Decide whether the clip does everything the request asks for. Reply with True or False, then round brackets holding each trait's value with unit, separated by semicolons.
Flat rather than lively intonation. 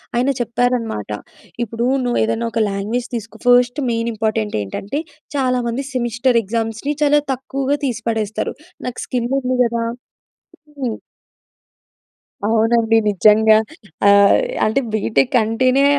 True (2.2 semitones)